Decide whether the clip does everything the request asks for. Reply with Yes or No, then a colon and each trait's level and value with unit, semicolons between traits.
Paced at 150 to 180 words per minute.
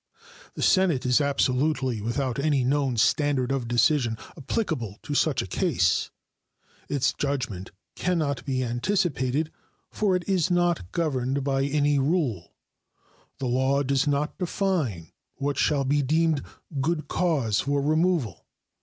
No: slow, 135 wpm